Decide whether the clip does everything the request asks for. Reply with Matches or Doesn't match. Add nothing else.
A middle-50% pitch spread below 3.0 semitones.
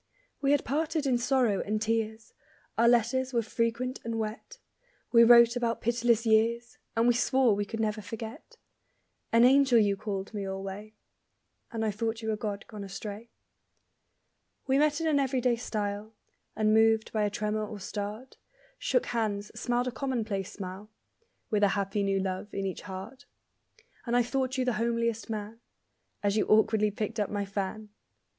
Matches